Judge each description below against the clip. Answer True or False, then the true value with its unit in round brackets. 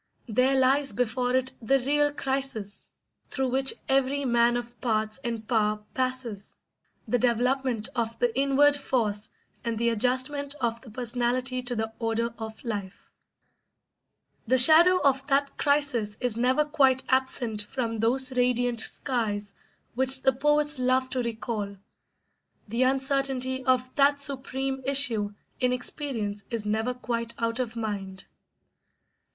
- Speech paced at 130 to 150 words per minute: True (135 wpm)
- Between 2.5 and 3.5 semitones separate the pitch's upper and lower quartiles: True (2.8 semitones)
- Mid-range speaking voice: False (250 Hz)